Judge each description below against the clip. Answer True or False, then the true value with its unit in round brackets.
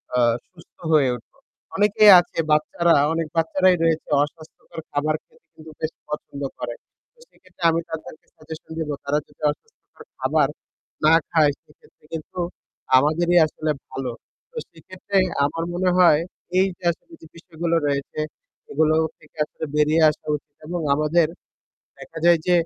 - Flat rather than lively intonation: True (2.3 semitones)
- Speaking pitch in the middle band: True (160 Hz)